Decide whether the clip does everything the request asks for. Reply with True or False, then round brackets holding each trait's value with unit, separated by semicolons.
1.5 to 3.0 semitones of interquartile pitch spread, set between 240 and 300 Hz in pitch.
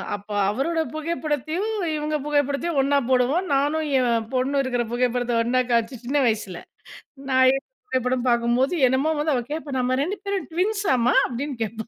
False (3.9 semitones; 265 Hz)